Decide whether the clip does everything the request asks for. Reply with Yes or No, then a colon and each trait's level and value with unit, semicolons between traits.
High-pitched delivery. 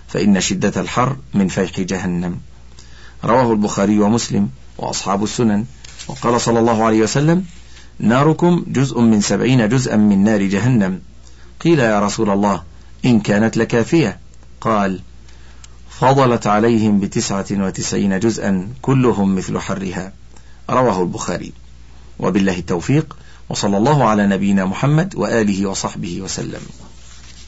No: low, 100 Hz